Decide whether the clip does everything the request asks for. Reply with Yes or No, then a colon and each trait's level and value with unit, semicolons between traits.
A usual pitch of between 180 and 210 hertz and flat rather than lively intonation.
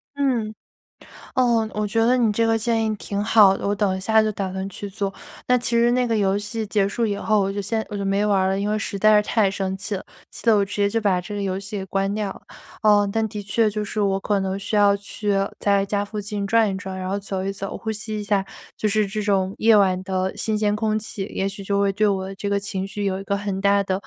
Yes: high, 205 Hz; narrow, 1.7 semitones